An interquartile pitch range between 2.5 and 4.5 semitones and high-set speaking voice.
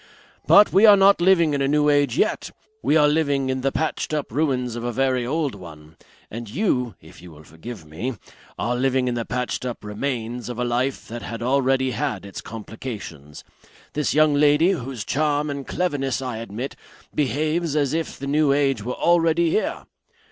No: average, 4.0 semitones; low, 135 Hz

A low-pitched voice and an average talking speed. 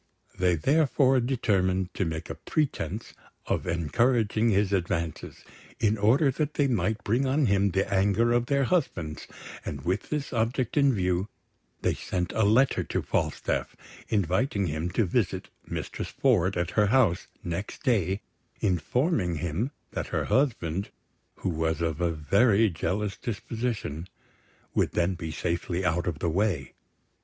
Yes: low, 100 Hz; average, 150 wpm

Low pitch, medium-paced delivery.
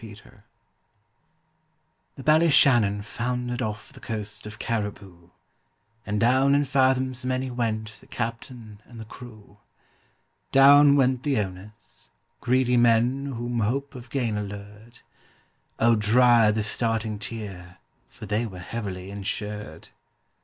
No: low, 115 Hz; slow, 115 wpm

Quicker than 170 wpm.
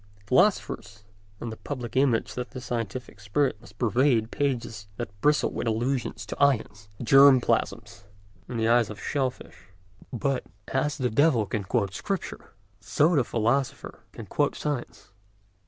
No: average, 150 wpm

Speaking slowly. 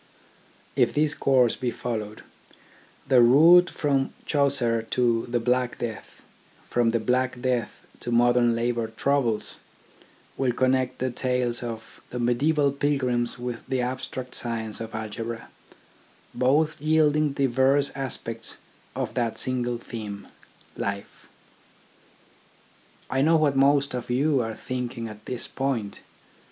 Yes: slow, 125 wpm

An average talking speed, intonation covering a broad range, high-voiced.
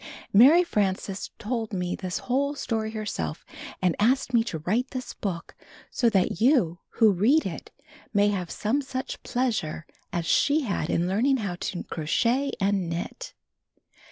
Yes: average, 155 wpm; wide, 5.9 semitones; high, 215 Hz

